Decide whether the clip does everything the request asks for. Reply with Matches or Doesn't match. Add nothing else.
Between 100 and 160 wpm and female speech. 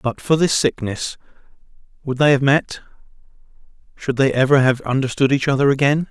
Doesn't match